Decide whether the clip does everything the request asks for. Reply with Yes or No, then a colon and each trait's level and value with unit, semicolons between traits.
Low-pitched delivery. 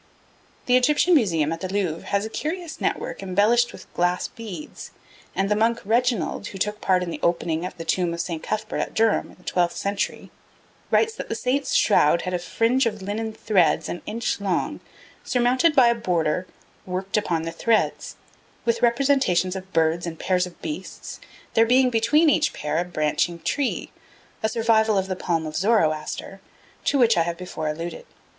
No: high, 195 Hz